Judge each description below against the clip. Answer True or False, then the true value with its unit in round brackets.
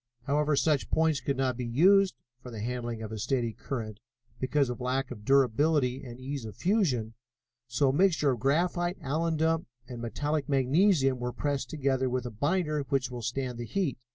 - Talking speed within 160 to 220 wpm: True (180 wpm)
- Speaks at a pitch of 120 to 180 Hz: True (135 Hz)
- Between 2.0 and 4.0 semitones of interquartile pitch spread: True (3.7 semitones)